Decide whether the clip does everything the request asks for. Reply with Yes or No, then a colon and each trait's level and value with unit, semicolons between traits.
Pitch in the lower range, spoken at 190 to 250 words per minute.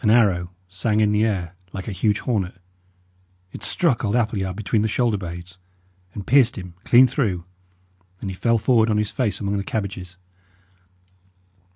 No: low, 105 Hz; average, 170 wpm